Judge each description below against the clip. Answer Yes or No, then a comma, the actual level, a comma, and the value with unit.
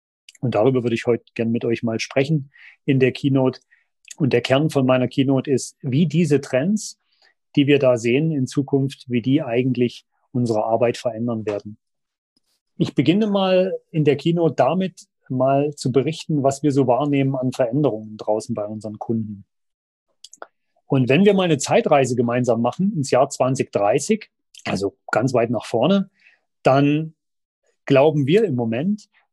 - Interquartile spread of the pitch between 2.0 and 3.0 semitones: No, average, 4.3 semitones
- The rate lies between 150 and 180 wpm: Yes, average, 160 wpm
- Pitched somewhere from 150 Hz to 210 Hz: No, low, 135 Hz